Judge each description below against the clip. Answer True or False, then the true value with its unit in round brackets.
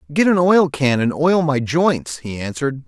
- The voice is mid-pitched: True (145 Hz)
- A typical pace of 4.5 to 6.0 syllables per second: True (4.6 syllables/s)